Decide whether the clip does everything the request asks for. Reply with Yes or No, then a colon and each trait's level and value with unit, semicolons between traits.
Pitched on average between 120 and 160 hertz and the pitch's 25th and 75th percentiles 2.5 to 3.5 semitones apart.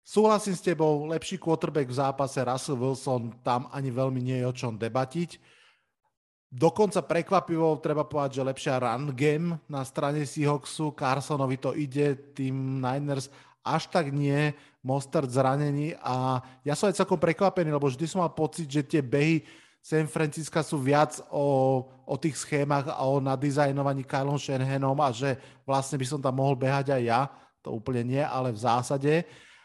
Yes: medium, 140 Hz; average, 2.9 semitones